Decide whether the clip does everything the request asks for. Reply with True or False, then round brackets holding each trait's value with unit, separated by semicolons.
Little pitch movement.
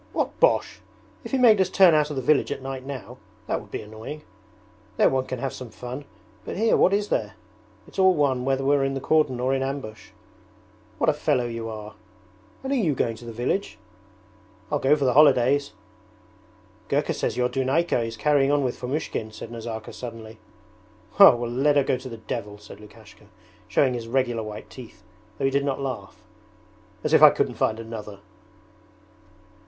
False (3.8 semitones)